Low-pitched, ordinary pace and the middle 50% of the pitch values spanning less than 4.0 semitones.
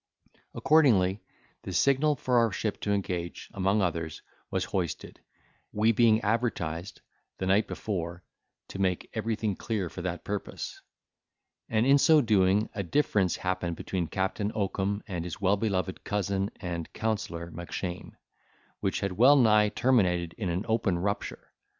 Yes: low, 100 Hz; average, 145 wpm; average, 3.4 semitones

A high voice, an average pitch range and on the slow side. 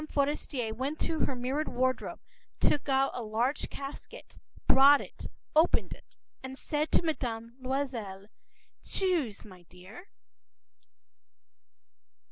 Yes: very high, 265 Hz; average, 4.1 semitones; slow, 110 wpm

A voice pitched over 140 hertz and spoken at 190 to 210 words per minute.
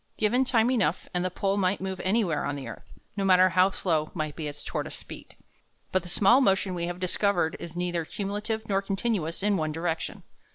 Yes: medium, 185 Hz; fast, 205 wpm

